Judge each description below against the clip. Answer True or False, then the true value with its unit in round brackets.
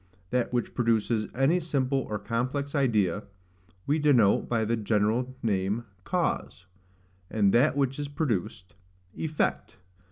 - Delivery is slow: True (125 wpm)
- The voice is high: False (120 Hz)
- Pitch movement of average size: True (4.6 semitones)